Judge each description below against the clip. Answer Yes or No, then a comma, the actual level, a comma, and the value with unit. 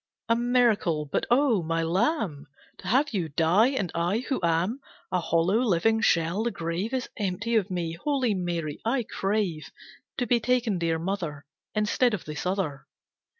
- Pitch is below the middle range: No, high, 195 Hz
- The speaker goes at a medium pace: Yes, average, 165 wpm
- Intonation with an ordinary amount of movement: No, wide, 5.8 semitones